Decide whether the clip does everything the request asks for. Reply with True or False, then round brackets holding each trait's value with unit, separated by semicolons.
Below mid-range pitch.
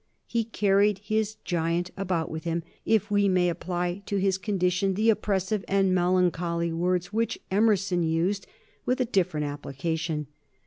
False (185 Hz)